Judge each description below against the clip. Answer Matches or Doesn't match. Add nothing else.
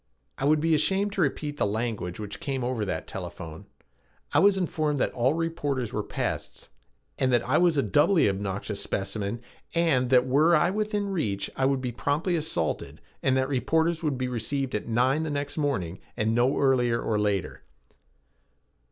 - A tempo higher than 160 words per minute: Matches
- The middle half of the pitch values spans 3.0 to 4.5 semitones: Doesn't match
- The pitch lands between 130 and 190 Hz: Matches